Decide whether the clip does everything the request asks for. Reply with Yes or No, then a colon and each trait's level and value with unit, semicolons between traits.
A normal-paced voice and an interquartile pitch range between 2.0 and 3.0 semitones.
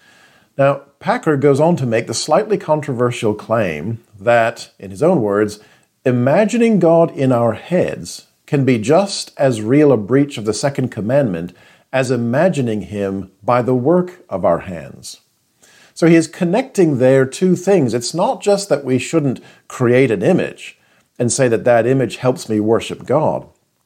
No: average, 165 wpm; average, 5.2 semitones